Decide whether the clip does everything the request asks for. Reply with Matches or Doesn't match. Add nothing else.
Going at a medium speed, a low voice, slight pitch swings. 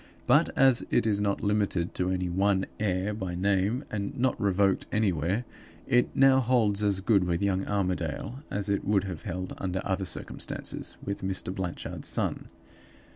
Matches